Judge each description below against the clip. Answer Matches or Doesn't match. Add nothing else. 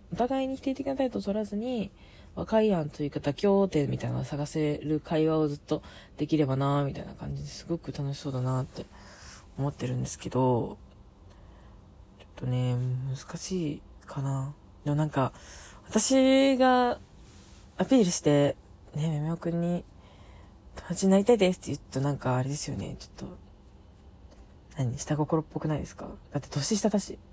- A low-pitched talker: Doesn't match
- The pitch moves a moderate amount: Doesn't match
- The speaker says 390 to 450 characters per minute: Doesn't match